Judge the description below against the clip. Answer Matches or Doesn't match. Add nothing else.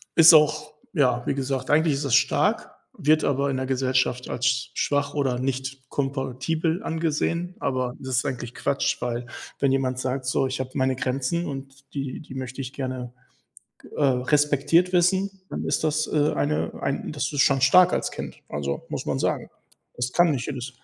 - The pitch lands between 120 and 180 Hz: Matches